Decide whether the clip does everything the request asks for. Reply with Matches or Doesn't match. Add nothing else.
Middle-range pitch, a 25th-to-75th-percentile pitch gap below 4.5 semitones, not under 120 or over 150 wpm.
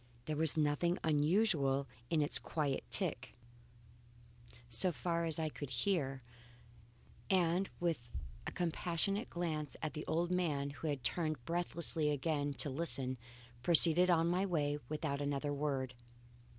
Matches